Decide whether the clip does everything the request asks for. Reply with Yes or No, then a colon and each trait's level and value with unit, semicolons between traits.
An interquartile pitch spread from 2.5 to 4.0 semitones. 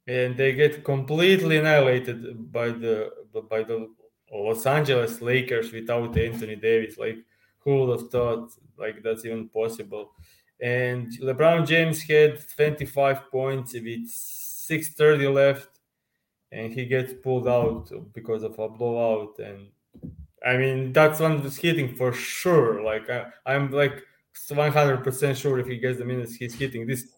Yes: average, 3.4 semitones